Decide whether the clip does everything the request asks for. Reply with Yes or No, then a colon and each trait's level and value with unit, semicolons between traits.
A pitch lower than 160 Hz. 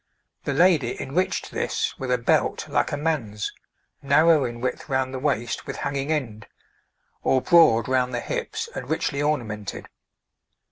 Yes: low, 135 Hz